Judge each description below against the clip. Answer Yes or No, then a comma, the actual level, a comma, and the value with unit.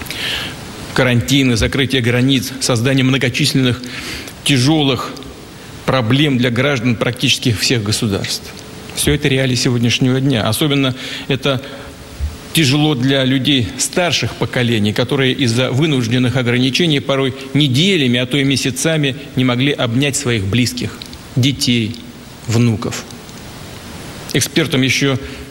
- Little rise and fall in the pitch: Yes, narrow, 2.0 semitones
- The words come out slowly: Yes, slow, 100 wpm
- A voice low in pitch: Yes, low, 130 Hz